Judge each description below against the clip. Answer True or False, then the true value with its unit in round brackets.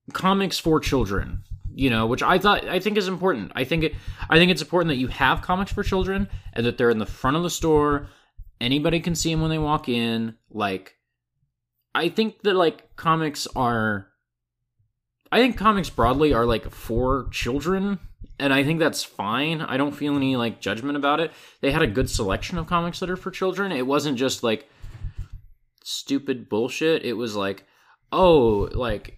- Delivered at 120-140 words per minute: False (190 wpm)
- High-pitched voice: False (135 Hz)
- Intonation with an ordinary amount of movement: False (6.4 semitones)